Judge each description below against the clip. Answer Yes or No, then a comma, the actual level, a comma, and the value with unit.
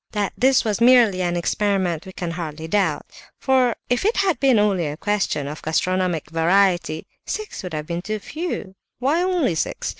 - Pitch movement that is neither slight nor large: No, wide, 6.5 semitones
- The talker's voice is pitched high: Yes, high, 195 Hz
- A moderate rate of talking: Yes, average, 180 wpm